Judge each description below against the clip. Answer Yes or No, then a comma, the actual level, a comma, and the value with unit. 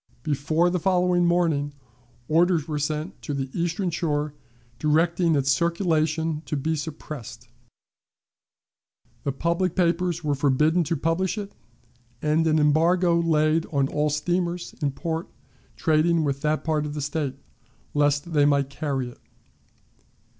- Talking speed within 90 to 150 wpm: Yes, slow, 135 wpm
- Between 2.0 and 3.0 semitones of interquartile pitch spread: Yes, narrow, 2.6 semitones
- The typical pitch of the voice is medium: Yes, medium, 155 Hz